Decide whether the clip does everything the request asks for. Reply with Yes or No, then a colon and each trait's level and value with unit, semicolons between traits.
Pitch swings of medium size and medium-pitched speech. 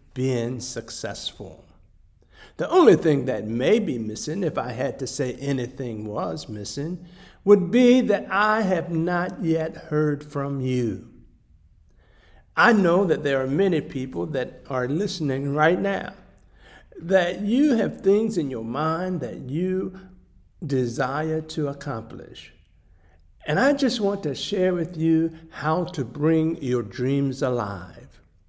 No: wide, 6.7 semitones; medium, 145 Hz